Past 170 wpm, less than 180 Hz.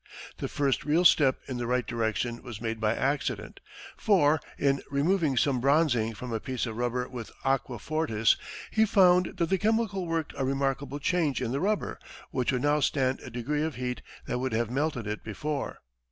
Yes: average, 190 wpm; low, 135 Hz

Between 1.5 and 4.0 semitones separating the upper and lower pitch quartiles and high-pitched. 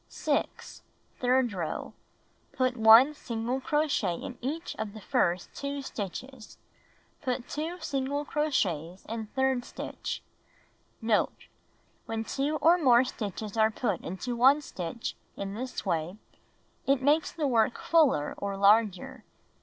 No: average, 4.7 semitones; high, 245 Hz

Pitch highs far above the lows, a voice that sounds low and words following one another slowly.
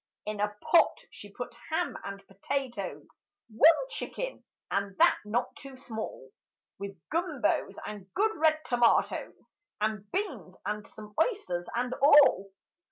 No: wide, 6.7 semitones; high, 230 Hz; slow, 130 wpm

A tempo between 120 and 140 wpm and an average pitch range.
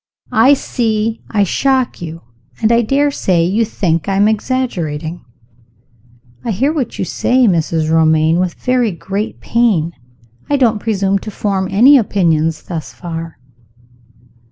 No: slow, 135 wpm; wide, 5.9 semitones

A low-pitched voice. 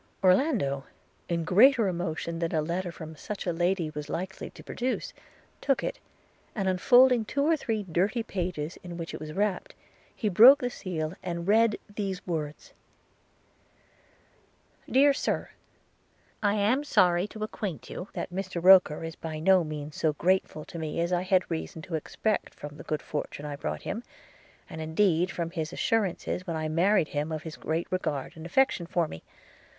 No: medium, 175 Hz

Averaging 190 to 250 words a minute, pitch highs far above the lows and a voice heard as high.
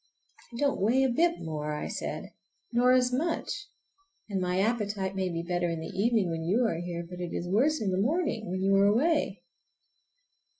Yes: average, 200 wpm; wide, 5.9 semitones; high, 200 Hz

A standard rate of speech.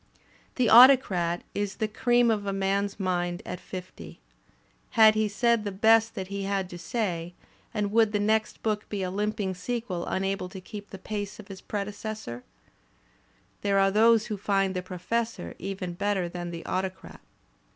Yes: average, 170 wpm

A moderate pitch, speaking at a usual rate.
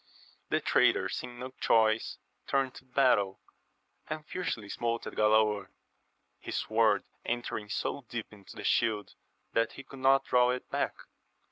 No: low, 115 Hz; average, 145 wpm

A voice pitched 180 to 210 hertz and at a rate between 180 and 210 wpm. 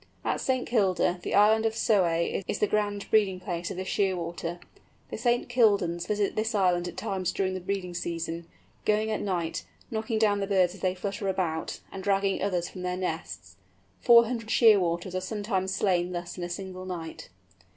Yes: high, 190 Hz; average, 185 wpm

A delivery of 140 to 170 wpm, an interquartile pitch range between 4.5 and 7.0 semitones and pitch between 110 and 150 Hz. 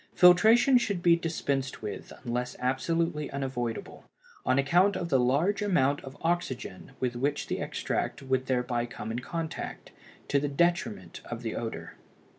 Yes: average, 150 wpm; wide, 5.6 semitones; medium, 140 Hz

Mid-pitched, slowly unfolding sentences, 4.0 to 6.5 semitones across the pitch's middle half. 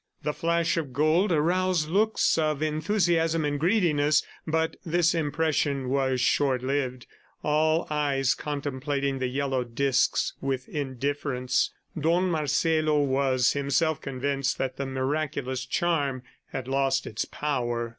No: medium, 145 Hz; slow, 125 wpm; average, 3.1 semitones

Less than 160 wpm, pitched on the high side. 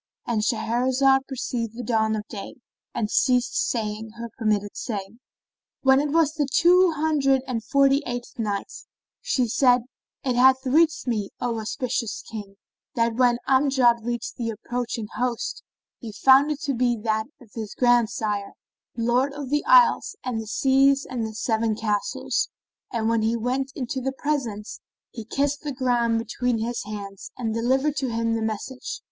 No: average, 165 wpm; high, 240 Hz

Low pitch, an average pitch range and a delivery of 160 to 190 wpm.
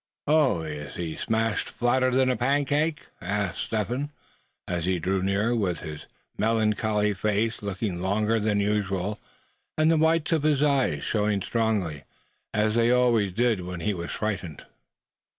No: low, 105 Hz; average, 4.5 semitones; average, 150 wpm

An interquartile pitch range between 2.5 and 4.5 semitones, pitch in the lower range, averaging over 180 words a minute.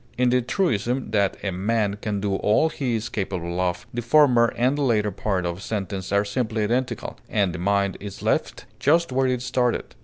Yes: average, 4.0 semitones; low, 105 Hz; fast, 205 wpm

